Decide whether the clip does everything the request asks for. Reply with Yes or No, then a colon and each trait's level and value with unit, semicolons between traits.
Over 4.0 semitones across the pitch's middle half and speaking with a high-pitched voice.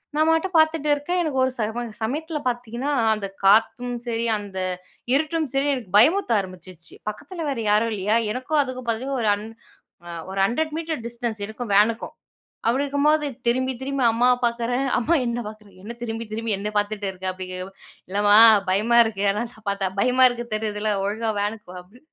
Yes: average, 4.5 semitones; high, 230 Hz